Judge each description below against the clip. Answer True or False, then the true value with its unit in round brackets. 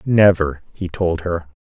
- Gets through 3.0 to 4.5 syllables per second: True (3.9 syllables/s)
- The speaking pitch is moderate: False (85 Hz)